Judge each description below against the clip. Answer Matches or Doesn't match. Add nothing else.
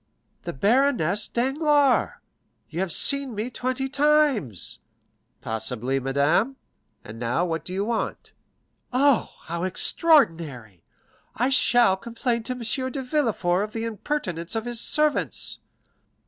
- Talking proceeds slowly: Matches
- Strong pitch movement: Matches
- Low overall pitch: Doesn't match